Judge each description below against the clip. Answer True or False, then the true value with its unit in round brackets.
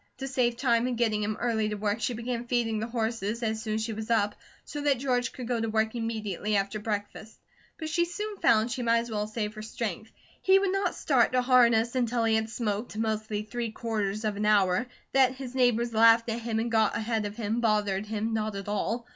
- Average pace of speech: False (230 wpm)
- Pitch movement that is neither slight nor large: False (2.1 semitones)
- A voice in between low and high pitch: False (225 Hz)